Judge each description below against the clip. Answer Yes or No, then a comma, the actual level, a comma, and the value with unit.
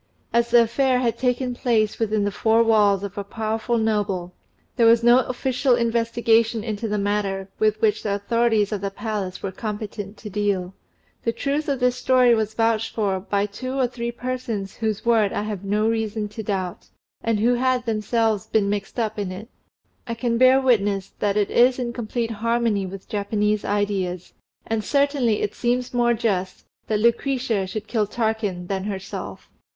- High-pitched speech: Yes, high, 220 Hz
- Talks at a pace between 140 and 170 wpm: No, average, 180 wpm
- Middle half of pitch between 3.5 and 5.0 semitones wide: No, average, 2.7 semitones